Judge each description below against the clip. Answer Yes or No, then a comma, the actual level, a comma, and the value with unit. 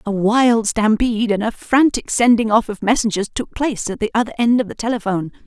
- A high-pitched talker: Yes, high, 225 Hz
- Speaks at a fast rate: Yes, fast, 210 wpm